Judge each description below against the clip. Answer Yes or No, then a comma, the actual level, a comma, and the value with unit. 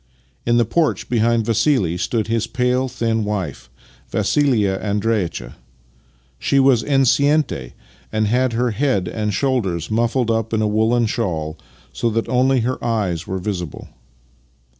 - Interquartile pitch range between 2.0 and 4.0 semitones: Yes, average, 3.7 semitones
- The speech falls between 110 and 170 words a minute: Yes, average, 140 wpm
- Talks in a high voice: No, low, 115 Hz